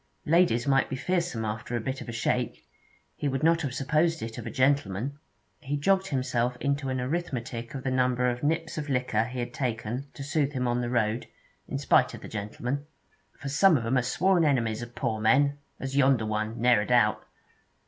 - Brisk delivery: Yes, fast, 210 wpm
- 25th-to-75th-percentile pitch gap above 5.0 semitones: No, average, 3.4 semitones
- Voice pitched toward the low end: Yes, low, 130 Hz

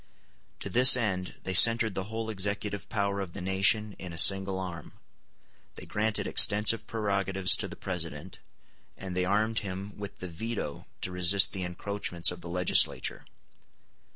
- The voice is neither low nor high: No, very low, 95 Hz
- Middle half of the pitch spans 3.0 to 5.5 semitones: No, narrow, 2.5 semitones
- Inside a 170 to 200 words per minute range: No, average, 155 wpm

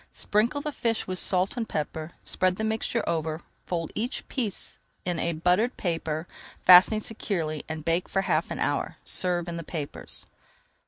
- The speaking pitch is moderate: Yes, medium, 180 Hz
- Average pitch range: Yes, average, 4.8 semitones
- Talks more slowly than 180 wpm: Yes, average, 160 wpm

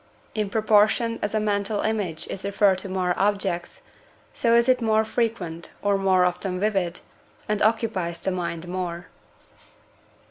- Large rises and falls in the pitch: No, average, 3.1 semitones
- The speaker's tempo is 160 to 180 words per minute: No, average, 145 wpm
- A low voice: No, high, 200 Hz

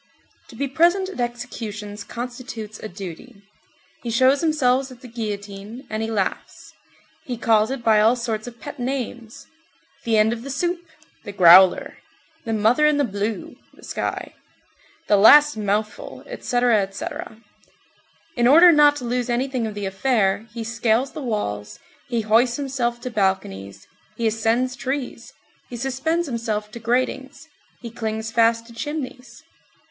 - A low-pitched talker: No, high, 235 Hz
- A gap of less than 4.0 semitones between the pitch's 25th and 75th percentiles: Yes, average, 3.3 semitones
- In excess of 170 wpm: No, average, 150 wpm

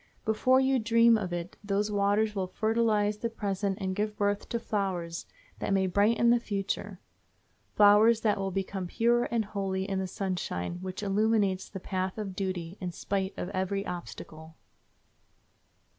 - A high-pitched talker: Yes, high, 200 Hz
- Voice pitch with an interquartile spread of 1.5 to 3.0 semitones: Yes, narrow, 2.4 semitones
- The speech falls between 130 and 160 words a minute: Yes, average, 155 wpm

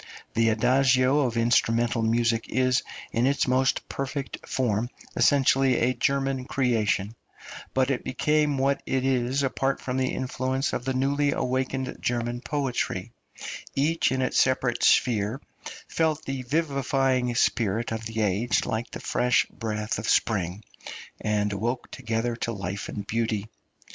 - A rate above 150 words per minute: No, average, 140 wpm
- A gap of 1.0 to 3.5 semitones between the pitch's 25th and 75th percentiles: Yes, average, 2.7 semitones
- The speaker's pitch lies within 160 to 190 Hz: No, low, 125 Hz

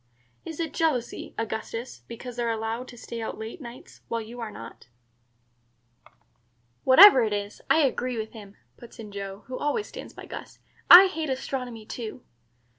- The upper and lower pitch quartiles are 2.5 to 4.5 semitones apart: Yes, average, 2.9 semitones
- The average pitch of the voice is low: No, high, 235 Hz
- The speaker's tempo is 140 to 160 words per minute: No, average, 170 wpm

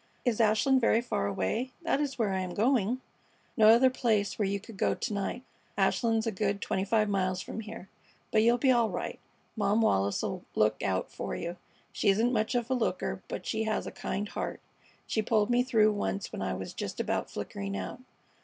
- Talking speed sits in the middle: No, fast, 210 wpm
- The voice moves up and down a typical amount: Yes, average, 3.4 semitones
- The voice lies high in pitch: Yes, high, 220 Hz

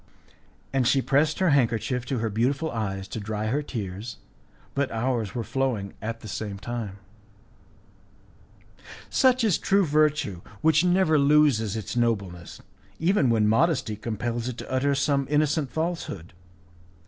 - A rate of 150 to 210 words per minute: No, average, 140 wpm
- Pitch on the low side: Yes, low, 125 Hz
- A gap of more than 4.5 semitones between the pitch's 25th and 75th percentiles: Yes, wide, 5.4 semitones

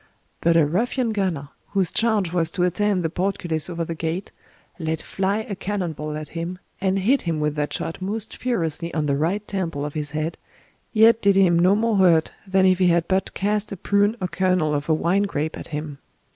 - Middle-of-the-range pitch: Yes, medium, 180 Hz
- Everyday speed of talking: No, fast, 215 wpm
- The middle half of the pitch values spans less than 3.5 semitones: No, average, 3.8 semitones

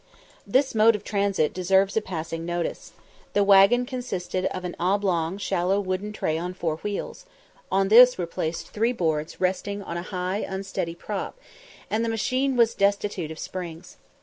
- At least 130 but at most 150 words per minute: No, average, 160 wpm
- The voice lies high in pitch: Yes, high, 195 Hz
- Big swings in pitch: No, average, 3.1 semitones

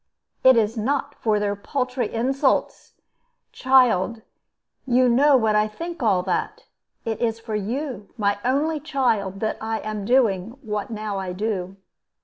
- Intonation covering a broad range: No, average, 3.8 semitones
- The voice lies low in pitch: No, high, 225 Hz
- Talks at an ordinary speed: Yes, average, 145 wpm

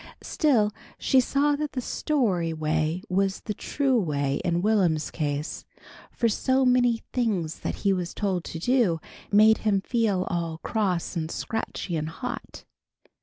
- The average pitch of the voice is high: Yes, high, 195 Hz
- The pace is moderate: Yes, average, 150 wpm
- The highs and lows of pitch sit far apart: Yes, wide, 6.4 semitones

